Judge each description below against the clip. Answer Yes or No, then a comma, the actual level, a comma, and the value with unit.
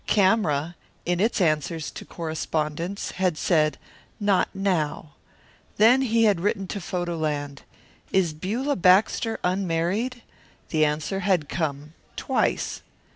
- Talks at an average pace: No, slow, 120 wpm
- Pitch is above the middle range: No, medium, 175 Hz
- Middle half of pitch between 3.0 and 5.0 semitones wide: Yes, average, 4.5 semitones